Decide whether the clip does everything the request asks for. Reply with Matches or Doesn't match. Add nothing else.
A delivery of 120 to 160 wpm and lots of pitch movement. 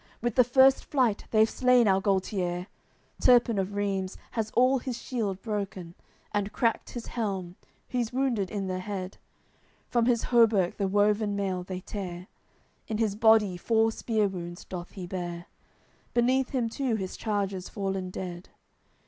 Doesn't match